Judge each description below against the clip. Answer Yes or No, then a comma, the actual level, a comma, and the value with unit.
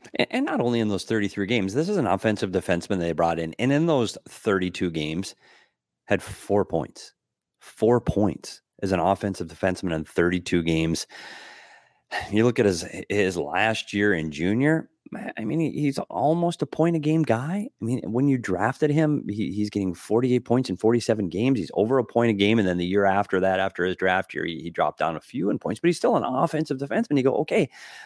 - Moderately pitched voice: No, low, 105 Hz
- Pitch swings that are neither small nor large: No, wide, 6.8 semitones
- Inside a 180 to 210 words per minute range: Yes, fast, 205 wpm